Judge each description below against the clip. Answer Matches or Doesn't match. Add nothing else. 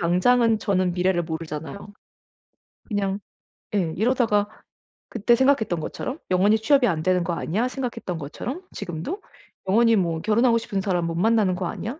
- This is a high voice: Matches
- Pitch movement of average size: Matches